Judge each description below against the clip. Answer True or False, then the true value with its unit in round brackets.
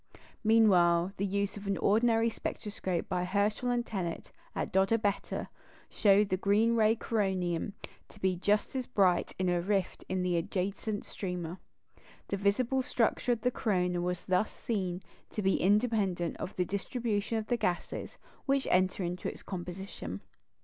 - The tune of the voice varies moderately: True (3.2 semitones)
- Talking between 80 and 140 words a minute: False (160 wpm)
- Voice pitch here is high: True (200 Hz)